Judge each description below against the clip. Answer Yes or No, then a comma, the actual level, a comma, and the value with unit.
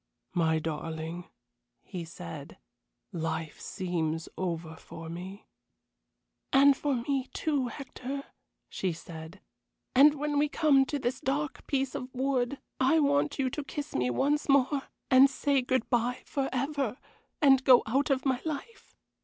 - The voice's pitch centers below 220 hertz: No, very high, 260 Hz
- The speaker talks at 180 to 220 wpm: No, average, 140 wpm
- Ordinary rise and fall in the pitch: No, wide, 8.0 semitones